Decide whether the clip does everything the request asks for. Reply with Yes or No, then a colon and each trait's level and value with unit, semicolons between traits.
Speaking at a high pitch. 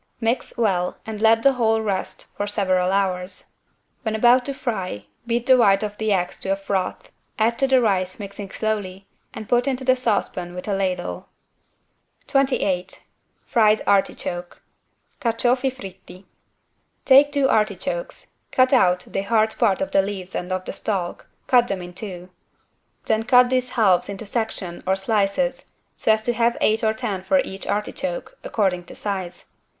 Yes: high, 210 Hz